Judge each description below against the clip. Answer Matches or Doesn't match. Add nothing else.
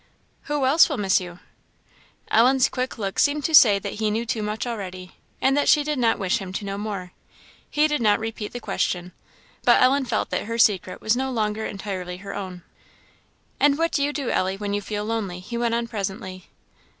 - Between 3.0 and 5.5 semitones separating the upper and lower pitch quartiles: Matches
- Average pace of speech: Doesn't match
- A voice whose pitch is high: Matches